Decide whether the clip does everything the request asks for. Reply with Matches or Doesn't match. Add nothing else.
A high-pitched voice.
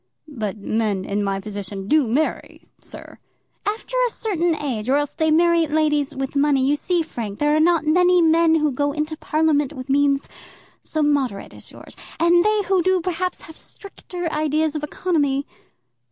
Matches